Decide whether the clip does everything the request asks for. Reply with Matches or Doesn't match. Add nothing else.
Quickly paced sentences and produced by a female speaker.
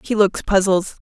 Doesn't match